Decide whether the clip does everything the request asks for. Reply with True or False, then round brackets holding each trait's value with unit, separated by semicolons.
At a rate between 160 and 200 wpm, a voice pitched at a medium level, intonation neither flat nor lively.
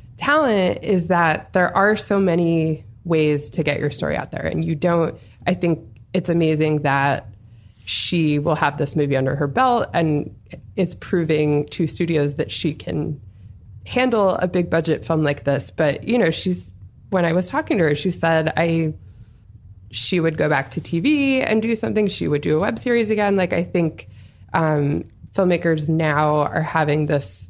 True (180 wpm; 160 Hz; 3.7 semitones)